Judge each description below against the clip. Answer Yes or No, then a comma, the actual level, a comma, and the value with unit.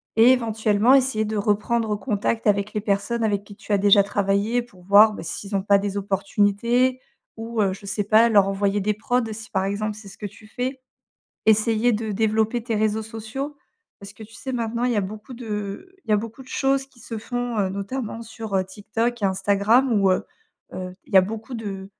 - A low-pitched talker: No, high, 215 Hz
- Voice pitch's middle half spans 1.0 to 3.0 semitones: Yes, narrow, 2.5 semitones